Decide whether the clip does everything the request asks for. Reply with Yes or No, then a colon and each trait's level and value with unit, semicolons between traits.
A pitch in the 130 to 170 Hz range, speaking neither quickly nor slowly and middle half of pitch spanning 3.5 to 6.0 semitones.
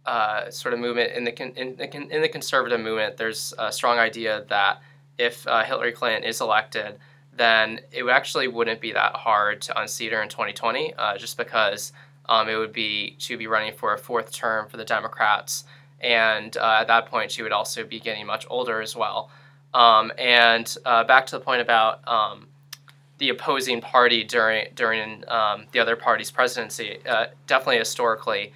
No: low, 120 Hz; average, 185 wpm; average, 3.9 semitones